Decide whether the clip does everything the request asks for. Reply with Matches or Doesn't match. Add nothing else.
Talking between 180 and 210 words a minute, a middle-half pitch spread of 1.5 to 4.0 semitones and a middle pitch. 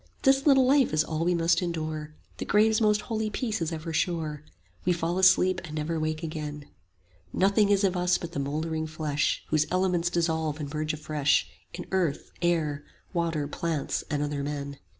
Matches